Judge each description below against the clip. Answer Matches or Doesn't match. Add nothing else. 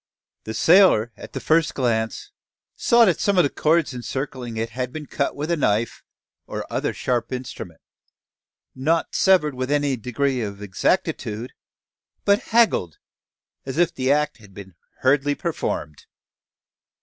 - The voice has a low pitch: Matches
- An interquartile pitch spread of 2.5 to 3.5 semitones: Doesn't match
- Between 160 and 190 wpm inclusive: Doesn't match